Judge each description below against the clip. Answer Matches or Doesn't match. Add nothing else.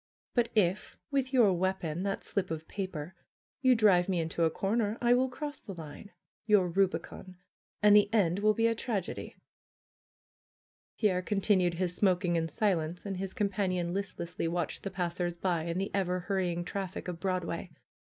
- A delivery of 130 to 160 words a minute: Doesn't match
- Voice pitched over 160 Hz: Matches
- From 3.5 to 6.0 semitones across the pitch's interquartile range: Doesn't match